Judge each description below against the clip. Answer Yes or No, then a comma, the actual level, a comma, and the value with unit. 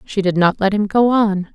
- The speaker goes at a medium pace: No, fast, 270 wpm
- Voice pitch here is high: Yes, high, 200 Hz